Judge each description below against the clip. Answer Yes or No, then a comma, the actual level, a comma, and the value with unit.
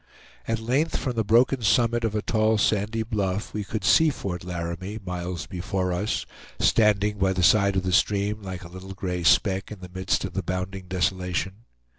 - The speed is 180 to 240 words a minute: Yes, average, 190 wpm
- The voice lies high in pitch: No, very low, 95 Hz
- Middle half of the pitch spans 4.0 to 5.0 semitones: No, average, 2.8 semitones